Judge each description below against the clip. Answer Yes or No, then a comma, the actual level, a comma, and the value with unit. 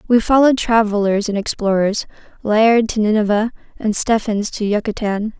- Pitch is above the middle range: Yes, high, 215 Hz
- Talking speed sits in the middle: No, slow, 120 wpm